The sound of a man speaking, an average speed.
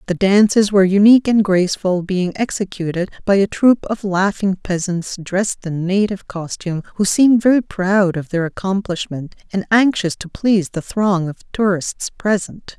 No: female; average, 160 wpm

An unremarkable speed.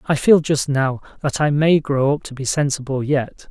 No: fast, 225 wpm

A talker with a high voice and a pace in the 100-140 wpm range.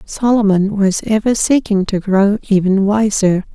Yes: high, 205 Hz; slow, 135 wpm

